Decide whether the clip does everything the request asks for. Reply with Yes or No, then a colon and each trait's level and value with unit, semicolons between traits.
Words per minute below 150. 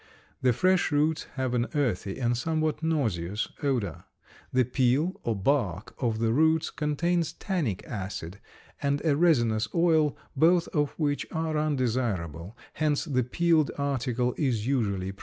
Yes: average, 140 wpm